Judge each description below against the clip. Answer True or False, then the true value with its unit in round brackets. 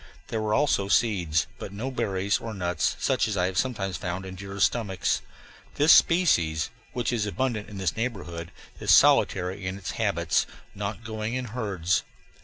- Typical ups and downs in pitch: True (3.7 semitones)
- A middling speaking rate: True (170 wpm)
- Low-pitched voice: True (100 Hz)